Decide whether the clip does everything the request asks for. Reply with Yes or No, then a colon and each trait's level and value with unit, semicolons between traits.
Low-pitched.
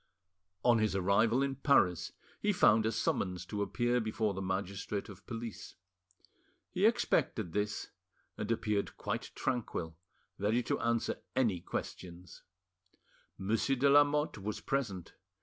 Yes: low, 110 Hz